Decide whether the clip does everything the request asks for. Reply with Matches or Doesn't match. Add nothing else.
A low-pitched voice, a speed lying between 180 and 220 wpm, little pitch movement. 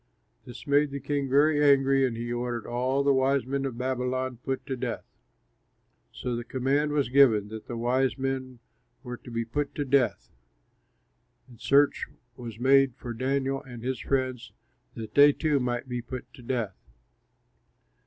Doesn't match